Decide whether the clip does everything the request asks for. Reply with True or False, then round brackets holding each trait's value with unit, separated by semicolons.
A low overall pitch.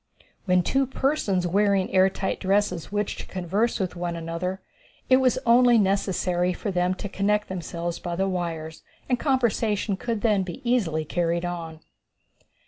False (190 Hz)